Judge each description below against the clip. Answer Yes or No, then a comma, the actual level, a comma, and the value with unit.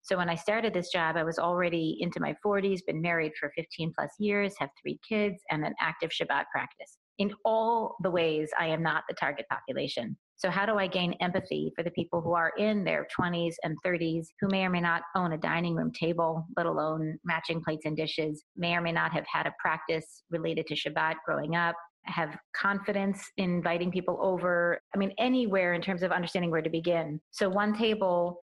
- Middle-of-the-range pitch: Yes, medium, 175 Hz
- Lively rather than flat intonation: No, average, 2.8 semitones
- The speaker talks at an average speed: No, fast, 210 wpm